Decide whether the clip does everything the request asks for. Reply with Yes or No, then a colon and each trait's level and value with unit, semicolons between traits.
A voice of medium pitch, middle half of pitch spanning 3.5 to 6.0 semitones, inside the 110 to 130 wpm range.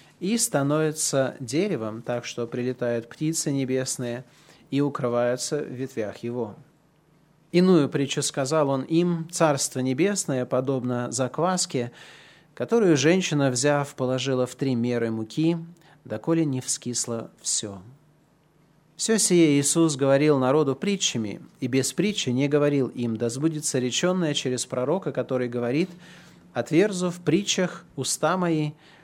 Yes: medium, 145 Hz; average, 4.2 semitones; average, 120 wpm